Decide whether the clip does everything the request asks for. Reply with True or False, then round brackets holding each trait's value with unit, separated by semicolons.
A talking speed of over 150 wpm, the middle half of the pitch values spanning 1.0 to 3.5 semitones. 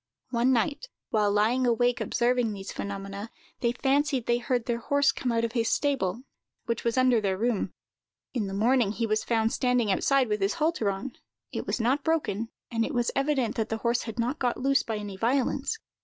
True (200 wpm; 3.0 semitones)